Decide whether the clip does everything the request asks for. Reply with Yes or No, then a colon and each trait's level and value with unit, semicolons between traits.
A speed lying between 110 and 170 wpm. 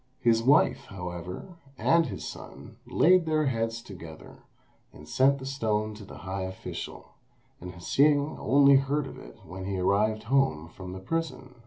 Yes: average, 160 wpm